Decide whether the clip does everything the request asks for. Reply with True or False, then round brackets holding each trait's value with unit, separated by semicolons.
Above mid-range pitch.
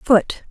True (210 Hz)